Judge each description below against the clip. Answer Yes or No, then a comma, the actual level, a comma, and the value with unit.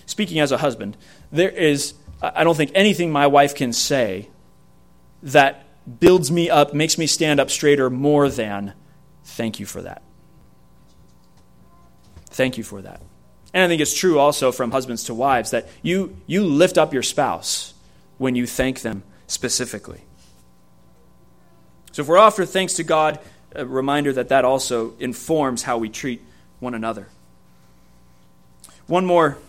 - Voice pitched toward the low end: Yes, low, 130 Hz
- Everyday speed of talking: Yes, average, 155 wpm